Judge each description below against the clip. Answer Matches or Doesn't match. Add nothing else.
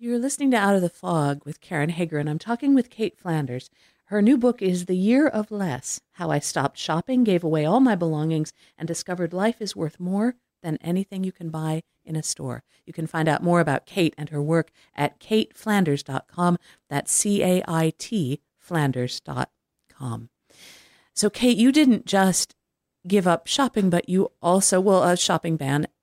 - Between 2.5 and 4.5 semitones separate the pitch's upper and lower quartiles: Doesn't match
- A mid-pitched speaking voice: Matches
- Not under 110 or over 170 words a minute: Doesn't match